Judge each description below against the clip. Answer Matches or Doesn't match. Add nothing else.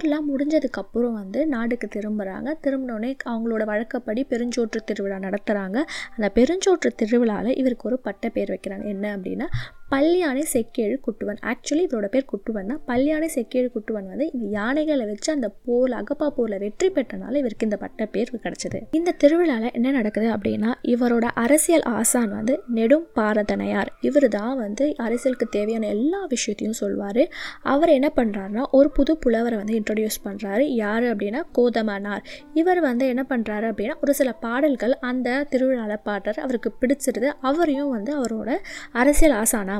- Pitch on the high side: Matches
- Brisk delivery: Matches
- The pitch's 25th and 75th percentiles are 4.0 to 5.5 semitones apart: Matches